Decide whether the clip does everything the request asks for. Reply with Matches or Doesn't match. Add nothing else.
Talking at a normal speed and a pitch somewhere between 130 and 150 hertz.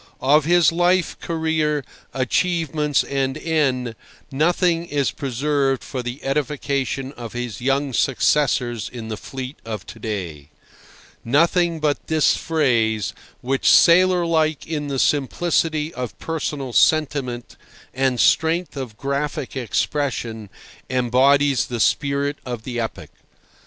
Doesn't match